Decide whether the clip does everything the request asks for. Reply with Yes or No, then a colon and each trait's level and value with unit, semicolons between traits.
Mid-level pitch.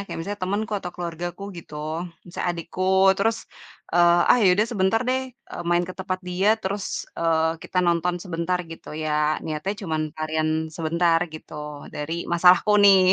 Yes: medium, 175 Hz